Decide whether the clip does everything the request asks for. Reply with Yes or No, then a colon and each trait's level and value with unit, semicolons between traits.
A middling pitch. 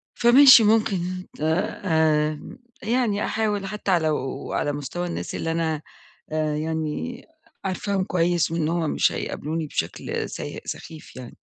Yes: medium, 170 Hz